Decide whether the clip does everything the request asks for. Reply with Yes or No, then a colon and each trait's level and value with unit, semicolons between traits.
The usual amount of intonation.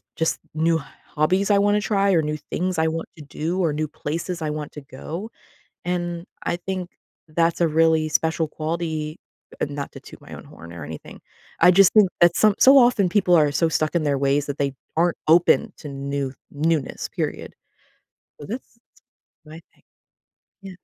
Yes: average, 3.1 semitones